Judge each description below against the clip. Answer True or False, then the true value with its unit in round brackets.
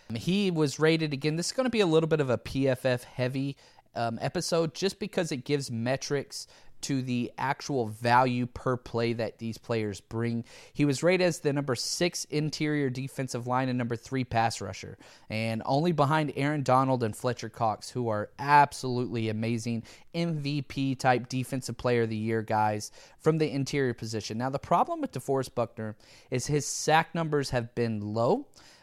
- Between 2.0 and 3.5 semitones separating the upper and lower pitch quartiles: False (4.1 semitones)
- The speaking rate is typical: True (175 wpm)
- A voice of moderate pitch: False (130 Hz)